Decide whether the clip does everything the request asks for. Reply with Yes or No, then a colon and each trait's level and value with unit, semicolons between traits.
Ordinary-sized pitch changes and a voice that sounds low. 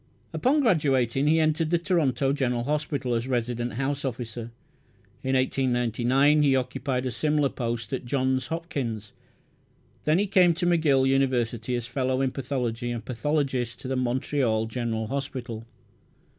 Yes: average, 3.1 semitones; low, 130 Hz